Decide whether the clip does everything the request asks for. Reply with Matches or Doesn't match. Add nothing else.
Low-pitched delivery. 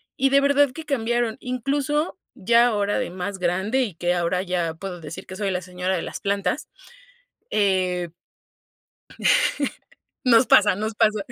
Doesn't match